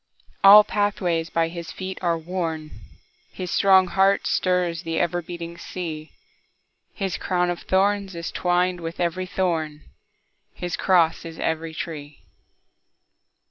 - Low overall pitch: No, medium, 175 Hz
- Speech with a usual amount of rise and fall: No, narrow, 2.2 semitones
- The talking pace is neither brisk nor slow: No, slow, 115 wpm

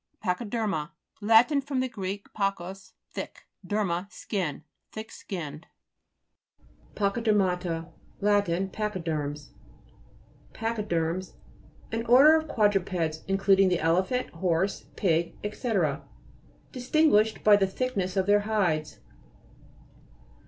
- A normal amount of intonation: Yes, average, 3.9 semitones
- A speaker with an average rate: No, slow, 105 wpm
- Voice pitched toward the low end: No, high, 195 Hz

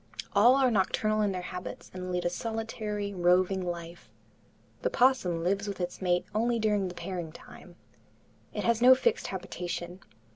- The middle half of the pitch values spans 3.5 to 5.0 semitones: Yes, average, 3.8 semitones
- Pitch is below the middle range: No, high, 195 Hz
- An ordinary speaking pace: Yes, average, 160 wpm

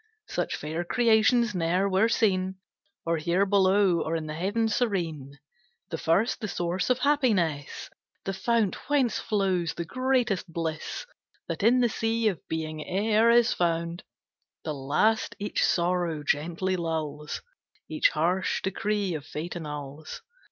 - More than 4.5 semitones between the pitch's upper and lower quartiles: Yes, average, 5.1 semitones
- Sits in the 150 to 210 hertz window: Yes, medium, 185 Hz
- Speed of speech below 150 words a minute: Yes, average, 140 wpm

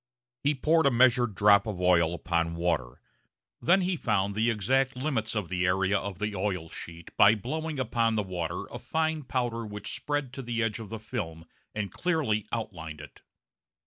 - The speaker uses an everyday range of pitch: No, wide, 5.7 semitones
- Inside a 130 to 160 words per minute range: No, average, 180 wpm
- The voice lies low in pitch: Yes, low, 110 Hz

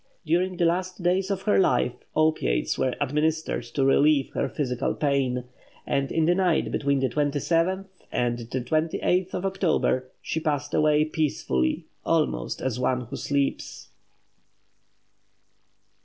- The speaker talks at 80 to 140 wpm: Yes, slow, 135 wpm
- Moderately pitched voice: Yes, medium, 150 Hz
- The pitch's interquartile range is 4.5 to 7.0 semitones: Yes, average, 4.9 semitones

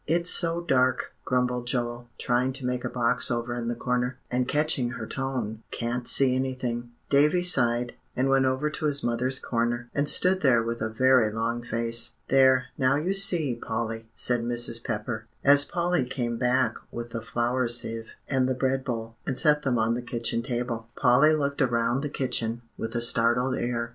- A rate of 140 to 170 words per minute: No, average, 185 wpm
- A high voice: No, low, 125 Hz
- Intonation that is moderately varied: No, narrow, 2.1 semitones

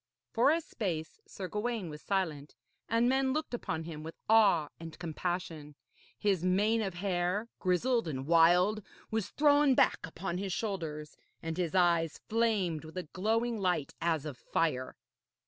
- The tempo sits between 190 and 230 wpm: No, average, 155 wpm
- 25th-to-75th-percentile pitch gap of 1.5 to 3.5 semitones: No, average, 5.3 semitones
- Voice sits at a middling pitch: Yes, medium, 180 Hz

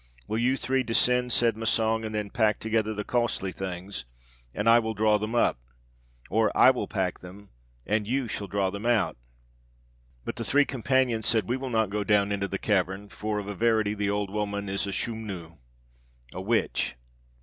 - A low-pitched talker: Yes, low, 105 Hz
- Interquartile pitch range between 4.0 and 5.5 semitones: No, narrow, 2.4 semitones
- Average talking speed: Yes, average, 190 wpm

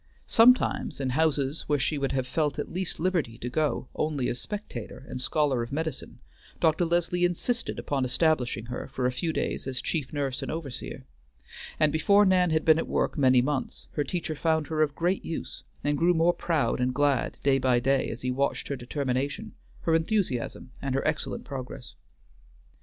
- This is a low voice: No, medium, 145 Hz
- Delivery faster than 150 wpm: Yes, average, 185 wpm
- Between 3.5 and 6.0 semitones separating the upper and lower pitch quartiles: Yes, average, 4.0 semitones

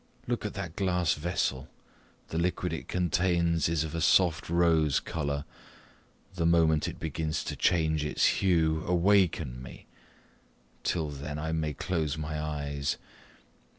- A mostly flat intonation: Yes, narrow, 2.2 semitones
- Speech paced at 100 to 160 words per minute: Yes, average, 140 wpm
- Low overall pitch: Yes, very low, 80 Hz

